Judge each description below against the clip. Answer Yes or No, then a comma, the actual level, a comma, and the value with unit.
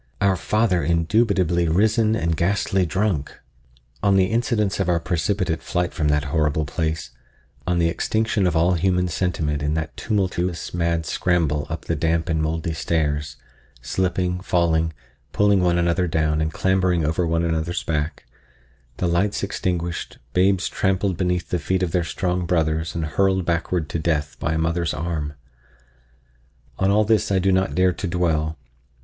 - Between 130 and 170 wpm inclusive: Yes, average, 155 wpm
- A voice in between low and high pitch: No, very low, 85 Hz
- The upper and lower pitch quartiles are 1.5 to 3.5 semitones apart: Yes, average, 2.9 semitones